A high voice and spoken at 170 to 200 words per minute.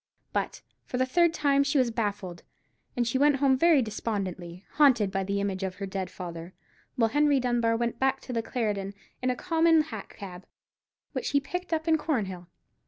Yes: high, 235 Hz; average, 190 wpm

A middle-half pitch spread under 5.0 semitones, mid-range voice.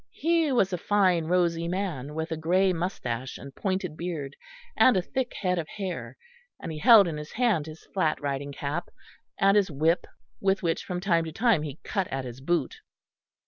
Yes: average, 4.2 semitones; medium, 170 Hz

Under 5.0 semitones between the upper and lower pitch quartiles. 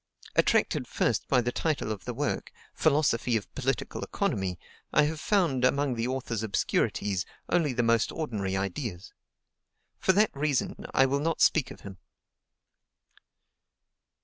No: wide, 5.5 semitones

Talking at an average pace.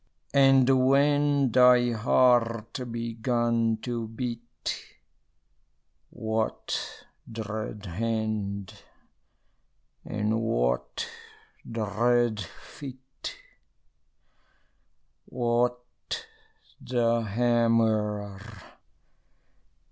No: slow, 50 wpm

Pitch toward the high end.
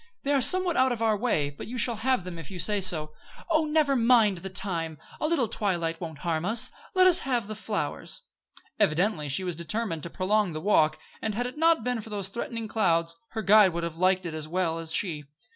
Yes: high, 200 Hz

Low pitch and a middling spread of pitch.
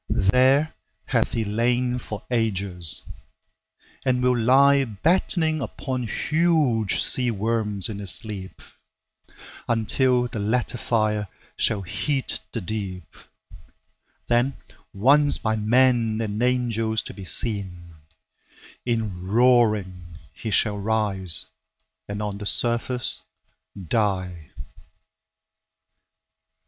Yes: low, 110 Hz; average, 3.8 semitones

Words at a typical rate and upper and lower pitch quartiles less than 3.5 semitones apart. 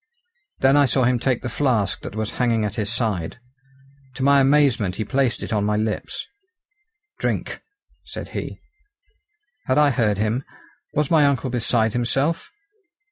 No: average, 155 wpm; average, 3.9 semitones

